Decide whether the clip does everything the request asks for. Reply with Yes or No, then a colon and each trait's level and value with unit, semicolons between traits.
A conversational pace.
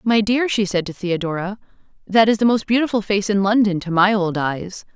No: fast, 220 wpm